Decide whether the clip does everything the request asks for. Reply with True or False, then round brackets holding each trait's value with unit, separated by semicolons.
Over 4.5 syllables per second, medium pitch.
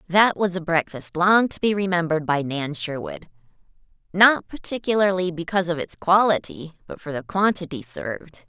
True (5.2 syllables/s; 170 Hz)